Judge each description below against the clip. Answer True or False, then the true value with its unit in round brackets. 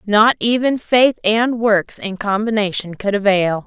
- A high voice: True (210 Hz)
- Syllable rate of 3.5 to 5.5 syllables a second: True (4.1 syllables/s)